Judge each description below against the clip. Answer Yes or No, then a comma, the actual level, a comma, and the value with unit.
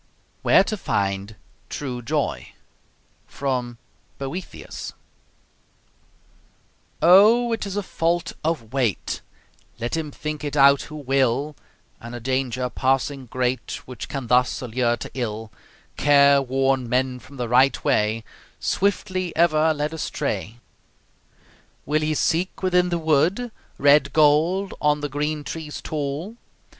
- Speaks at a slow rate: Yes, slow, 120 wpm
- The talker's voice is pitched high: No, medium, 140 Hz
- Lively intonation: No, average, 4.2 semitones